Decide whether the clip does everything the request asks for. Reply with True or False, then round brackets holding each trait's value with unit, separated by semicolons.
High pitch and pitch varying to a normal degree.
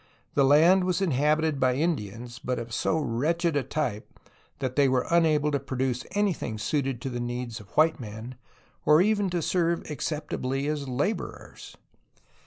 False (140 Hz; 4.5 semitones)